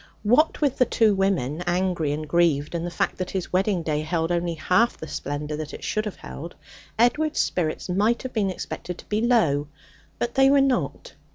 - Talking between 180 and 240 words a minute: Yes, average, 200 wpm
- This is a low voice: No, medium, 180 Hz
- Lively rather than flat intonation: Yes, wide, 6.2 semitones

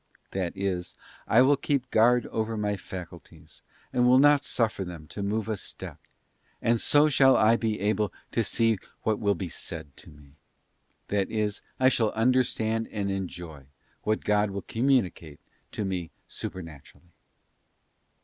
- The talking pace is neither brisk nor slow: Yes, average, 155 wpm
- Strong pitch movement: No, average, 3.8 semitones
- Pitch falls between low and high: No, low, 105 Hz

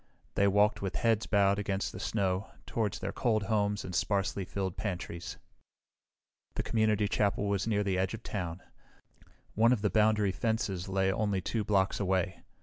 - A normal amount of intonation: No, narrow, 2.0 semitones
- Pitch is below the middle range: Yes, low, 100 Hz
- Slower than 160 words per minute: No, average, 165 wpm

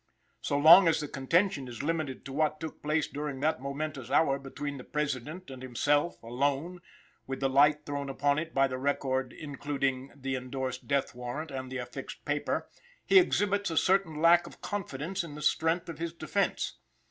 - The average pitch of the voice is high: No, medium, 145 Hz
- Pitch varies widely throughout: No, average, 3.2 semitones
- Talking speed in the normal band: Yes, average, 180 wpm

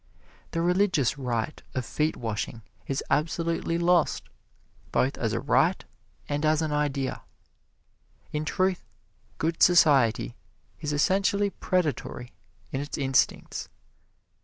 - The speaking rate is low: Yes, slow, 110 wpm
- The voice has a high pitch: No, medium, 150 Hz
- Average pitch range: Yes, average, 4.3 semitones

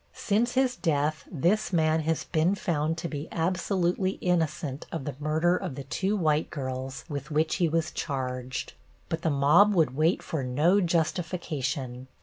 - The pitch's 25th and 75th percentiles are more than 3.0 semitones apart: Yes, average, 3.6 semitones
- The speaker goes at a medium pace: Yes, average, 160 wpm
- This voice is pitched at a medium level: Yes, medium, 160 Hz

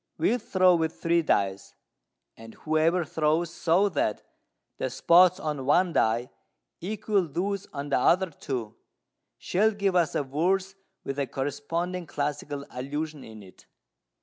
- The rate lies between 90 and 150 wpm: Yes, average, 140 wpm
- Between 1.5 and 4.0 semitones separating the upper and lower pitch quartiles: No, average, 4.5 semitones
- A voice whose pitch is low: No, medium, 160 Hz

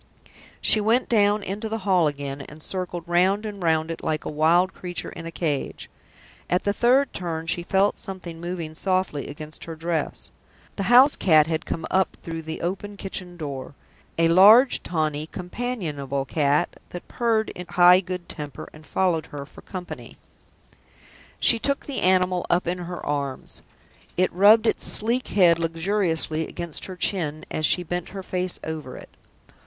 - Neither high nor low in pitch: Yes, medium, 175 Hz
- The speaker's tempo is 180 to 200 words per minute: No, average, 170 wpm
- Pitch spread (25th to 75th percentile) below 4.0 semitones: Yes, average, 3.5 semitones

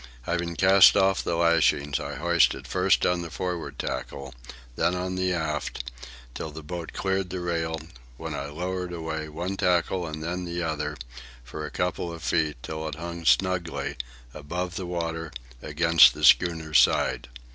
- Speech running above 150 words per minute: Yes, average, 165 wpm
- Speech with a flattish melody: Yes, narrow, 2.3 semitones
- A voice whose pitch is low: Yes, very low, 85 Hz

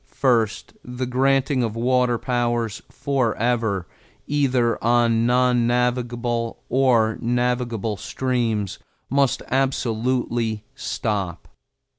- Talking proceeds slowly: Yes, slow, 85 wpm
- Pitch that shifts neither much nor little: No, narrow, 1.8 semitones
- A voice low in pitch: Yes, low, 120 Hz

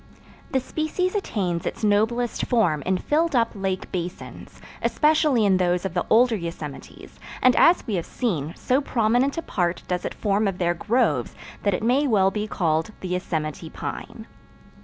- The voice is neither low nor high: No, high, 205 Hz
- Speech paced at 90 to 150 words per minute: No, average, 170 wpm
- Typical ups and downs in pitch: No, wide, 5.7 semitones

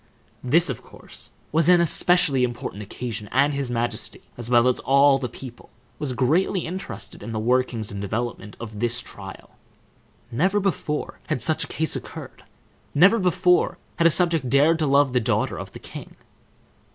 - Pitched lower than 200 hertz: Yes, low, 135 Hz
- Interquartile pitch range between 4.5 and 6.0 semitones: Yes, wide, 5.5 semitones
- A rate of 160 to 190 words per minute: Yes, average, 170 wpm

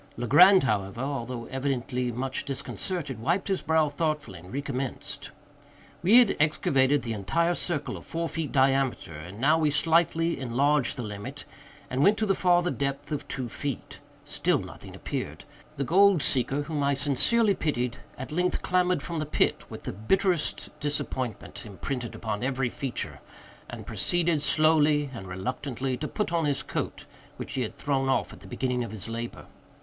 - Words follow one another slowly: No, average, 165 wpm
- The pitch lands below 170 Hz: Yes, medium, 140 Hz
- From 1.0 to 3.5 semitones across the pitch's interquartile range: No, average, 4.5 semitones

